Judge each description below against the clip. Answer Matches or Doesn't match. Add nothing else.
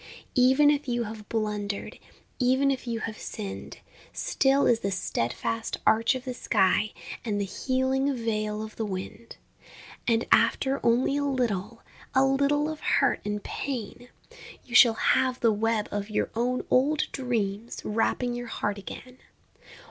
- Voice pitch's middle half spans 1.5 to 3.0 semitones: Doesn't match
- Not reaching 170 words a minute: Matches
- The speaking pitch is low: Doesn't match